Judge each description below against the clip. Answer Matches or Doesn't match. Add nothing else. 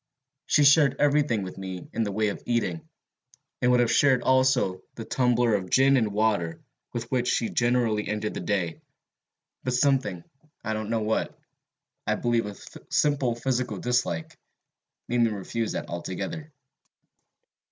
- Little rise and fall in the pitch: Doesn't match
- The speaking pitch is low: Matches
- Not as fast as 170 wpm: Matches